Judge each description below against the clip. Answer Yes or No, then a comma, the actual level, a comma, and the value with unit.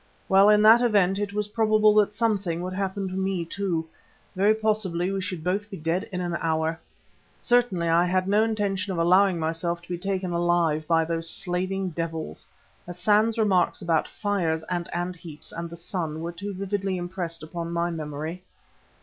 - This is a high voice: No, medium, 180 Hz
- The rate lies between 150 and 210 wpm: Yes, average, 180 wpm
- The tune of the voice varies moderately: Yes, average, 3.1 semitones